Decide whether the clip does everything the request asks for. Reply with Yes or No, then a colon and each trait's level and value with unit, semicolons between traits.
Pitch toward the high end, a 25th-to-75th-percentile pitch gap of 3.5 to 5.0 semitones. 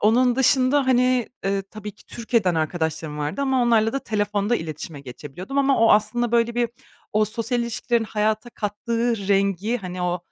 Yes: high, 220 Hz; average, 3.8 semitones